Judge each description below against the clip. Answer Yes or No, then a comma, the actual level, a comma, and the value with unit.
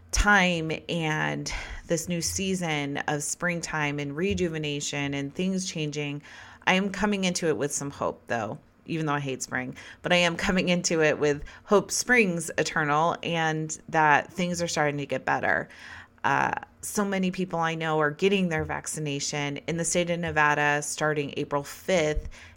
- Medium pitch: Yes, medium, 155 Hz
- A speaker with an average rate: Yes, average, 165 wpm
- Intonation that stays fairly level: No, average, 3.5 semitones